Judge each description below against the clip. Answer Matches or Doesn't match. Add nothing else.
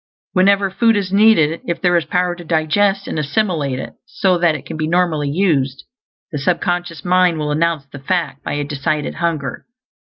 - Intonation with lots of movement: Doesn't match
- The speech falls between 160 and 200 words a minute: Matches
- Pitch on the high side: Doesn't match